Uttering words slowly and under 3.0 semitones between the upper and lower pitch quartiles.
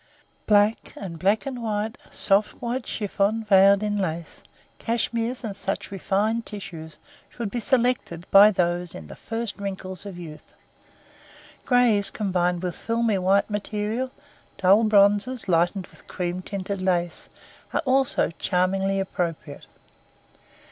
No: slow, 125 wpm; average, 3.4 semitones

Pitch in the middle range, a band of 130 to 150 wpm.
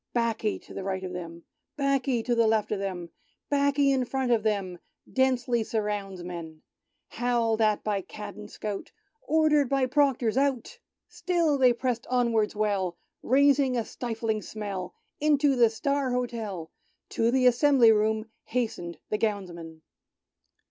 No: high, 230 Hz; average, 140 wpm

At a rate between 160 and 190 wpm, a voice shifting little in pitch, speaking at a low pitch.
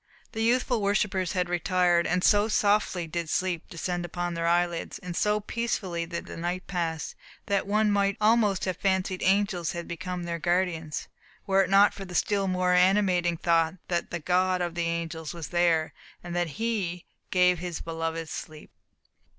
No: average, 175 wpm; narrow, 2.3 semitones; medium, 180 Hz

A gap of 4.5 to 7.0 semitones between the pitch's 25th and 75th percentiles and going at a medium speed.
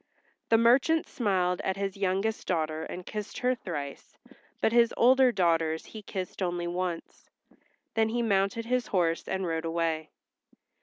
Yes: average, 5.0 semitones; average, 150 wpm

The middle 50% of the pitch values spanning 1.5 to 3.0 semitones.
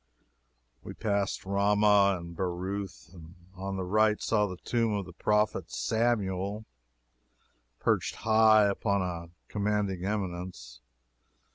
Yes: narrow, 2.5 semitones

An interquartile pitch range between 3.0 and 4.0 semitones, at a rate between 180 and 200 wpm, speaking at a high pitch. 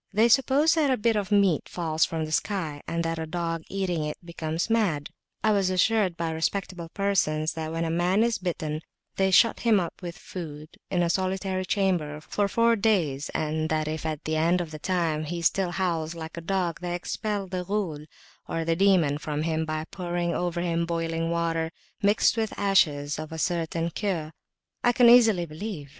No: average, 3.7 semitones; average, 190 wpm; medium, 170 Hz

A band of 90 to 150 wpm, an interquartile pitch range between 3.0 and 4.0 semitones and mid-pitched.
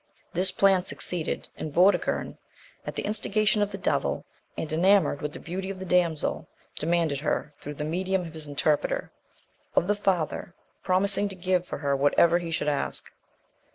No: average, 170 wpm; average, 3.6 semitones; medium, 175 Hz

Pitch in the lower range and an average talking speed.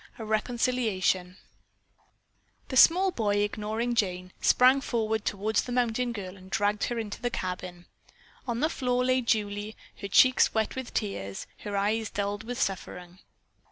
No: high, 215 Hz; average, 145 wpm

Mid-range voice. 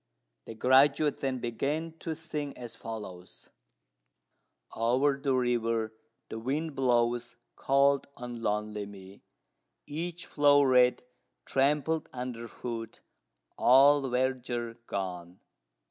No: low, 125 Hz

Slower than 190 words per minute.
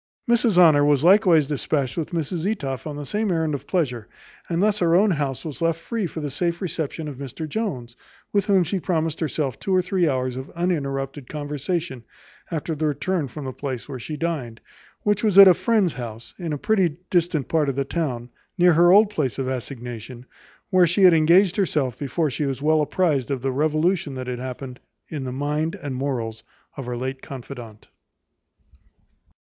No: average, 195 wpm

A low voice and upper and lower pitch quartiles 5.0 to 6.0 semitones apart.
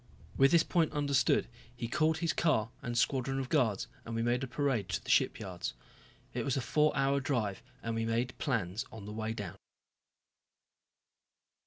No: low, 125 Hz; average, 3.8 semitones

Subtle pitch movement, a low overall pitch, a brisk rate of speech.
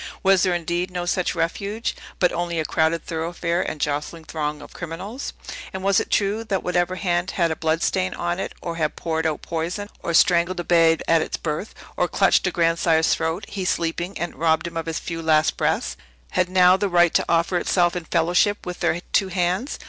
No: narrow, 2.0 semitones; medium, 175 Hz; fast, 210 wpm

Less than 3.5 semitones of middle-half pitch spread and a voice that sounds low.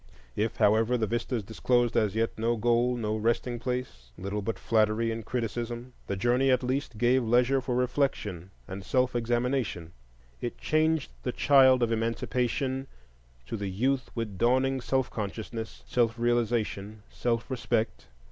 Yes: narrow, 2.4 semitones; low, 120 Hz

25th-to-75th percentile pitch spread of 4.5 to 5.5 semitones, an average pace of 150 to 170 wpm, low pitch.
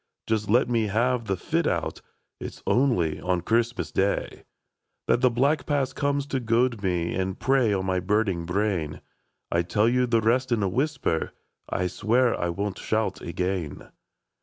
No: average, 5.1 semitones; average, 180 wpm; low, 110 Hz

